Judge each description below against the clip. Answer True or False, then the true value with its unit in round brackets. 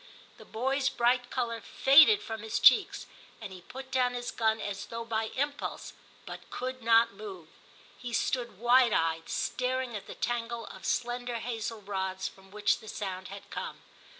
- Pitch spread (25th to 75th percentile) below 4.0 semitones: True (3.2 semitones)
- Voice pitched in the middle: False (235 Hz)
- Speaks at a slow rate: False (170 wpm)